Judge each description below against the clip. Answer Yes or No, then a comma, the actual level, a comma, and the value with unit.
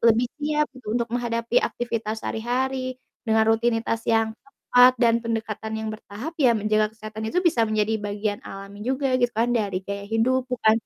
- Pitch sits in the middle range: No, high, 230 Hz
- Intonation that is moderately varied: No, narrow, 2.3 semitones